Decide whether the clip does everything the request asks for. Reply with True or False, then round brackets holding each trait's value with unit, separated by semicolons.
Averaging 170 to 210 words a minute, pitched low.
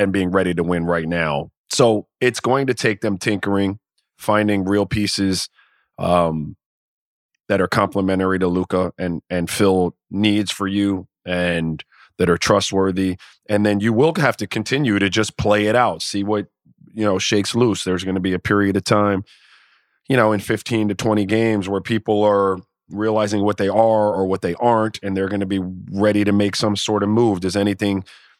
True (190 wpm; 100 Hz)